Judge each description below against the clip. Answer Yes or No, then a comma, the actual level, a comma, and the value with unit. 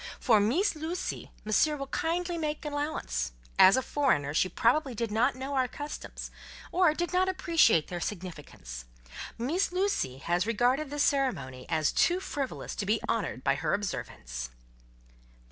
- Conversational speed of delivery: Yes, average, 150 wpm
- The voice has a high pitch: Yes, very high, 250 Hz